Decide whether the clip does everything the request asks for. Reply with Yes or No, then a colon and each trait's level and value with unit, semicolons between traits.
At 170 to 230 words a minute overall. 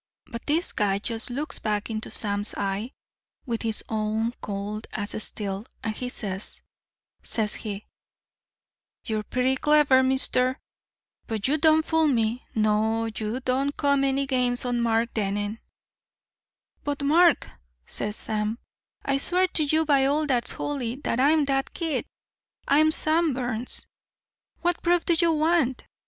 No: average, 145 wpm